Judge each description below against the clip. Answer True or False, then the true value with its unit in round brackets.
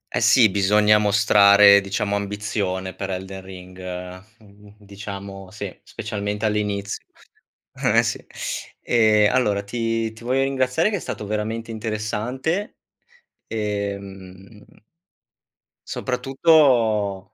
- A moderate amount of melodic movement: False (2.3 semitones)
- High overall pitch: False (105 Hz)